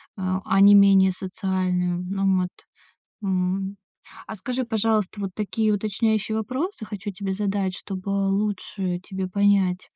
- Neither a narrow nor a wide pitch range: No, narrow, 2.0 semitones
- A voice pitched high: Yes, high, 195 Hz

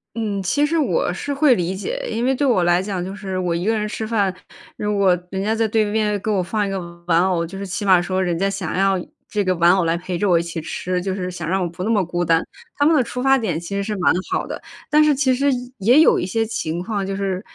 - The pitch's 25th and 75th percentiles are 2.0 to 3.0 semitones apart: No, average, 3.7 semitones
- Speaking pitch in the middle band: No, high, 195 Hz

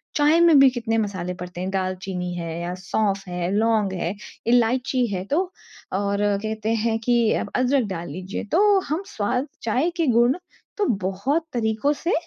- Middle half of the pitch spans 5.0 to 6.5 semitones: Yes, average, 5.3 semitones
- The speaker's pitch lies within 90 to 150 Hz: No, high, 220 Hz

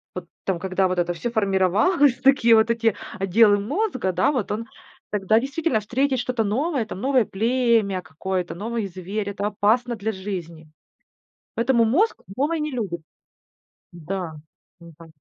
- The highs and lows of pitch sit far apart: No, average, 4.6 semitones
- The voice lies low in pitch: No, high, 215 Hz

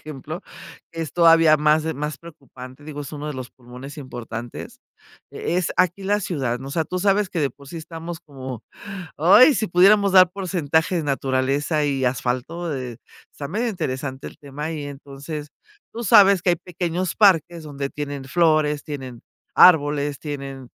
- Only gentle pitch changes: No, average, 4.1 semitones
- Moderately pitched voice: Yes, medium, 150 Hz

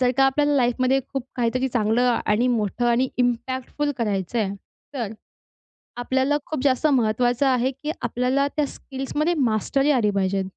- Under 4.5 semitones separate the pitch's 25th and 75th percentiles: Yes, narrow, 2.5 semitones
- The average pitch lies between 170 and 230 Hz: No, very high, 250 Hz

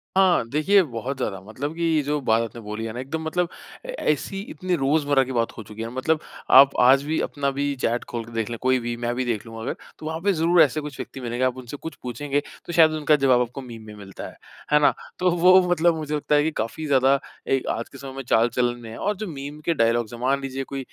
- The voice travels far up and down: No, average, 4.5 semitones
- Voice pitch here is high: No, low, 135 Hz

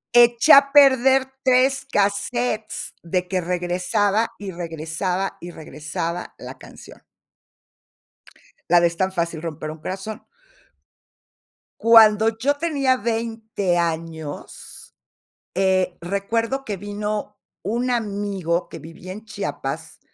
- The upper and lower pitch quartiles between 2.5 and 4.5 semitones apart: No, average, 4.9 semitones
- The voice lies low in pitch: No, high, 200 Hz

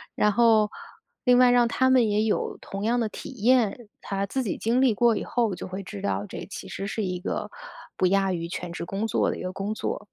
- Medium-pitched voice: No, high, 210 Hz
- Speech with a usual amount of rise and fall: Yes, average, 3.7 semitones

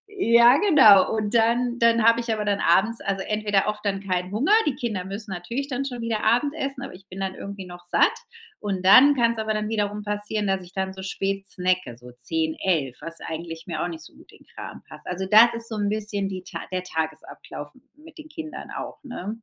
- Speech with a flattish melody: No, average, 3.9 semitones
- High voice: Yes, high, 205 Hz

